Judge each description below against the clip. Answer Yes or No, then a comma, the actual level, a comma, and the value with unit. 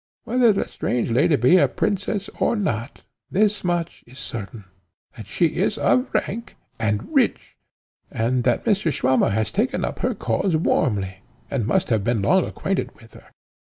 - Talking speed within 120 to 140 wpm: No, average, 165 wpm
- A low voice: Yes, low, 130 Hz